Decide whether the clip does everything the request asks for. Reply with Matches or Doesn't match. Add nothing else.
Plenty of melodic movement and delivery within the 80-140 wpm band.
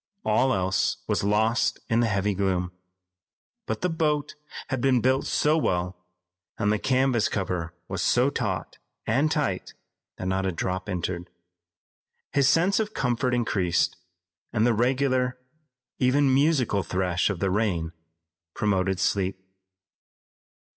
Matches